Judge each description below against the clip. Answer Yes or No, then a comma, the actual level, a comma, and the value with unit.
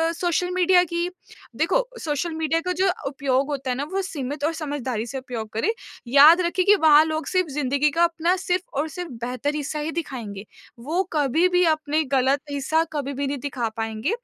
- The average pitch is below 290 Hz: No, very high, 300 Hz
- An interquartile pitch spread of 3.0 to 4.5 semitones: Yes, average, 4.1 semitones